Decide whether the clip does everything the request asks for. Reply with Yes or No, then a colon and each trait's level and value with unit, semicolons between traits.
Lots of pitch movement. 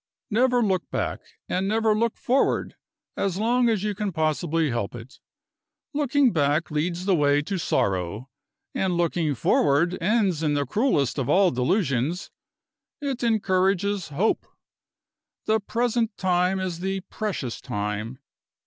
Yes: wide, 6.6 semitones